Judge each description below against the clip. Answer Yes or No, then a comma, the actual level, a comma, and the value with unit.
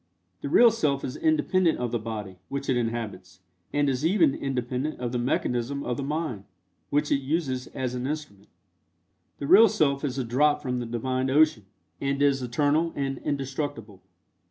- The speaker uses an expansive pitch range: No, average, 3.4 semitones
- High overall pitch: No, low, 135 Hz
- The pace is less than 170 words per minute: No, average, 175 wpm